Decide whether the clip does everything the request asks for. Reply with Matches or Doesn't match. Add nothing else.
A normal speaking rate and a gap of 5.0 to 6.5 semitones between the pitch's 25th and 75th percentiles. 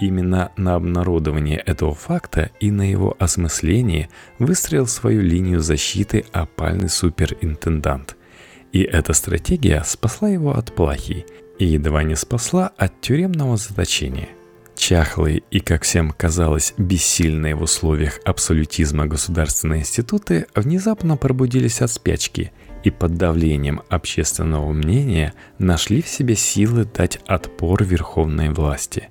Matches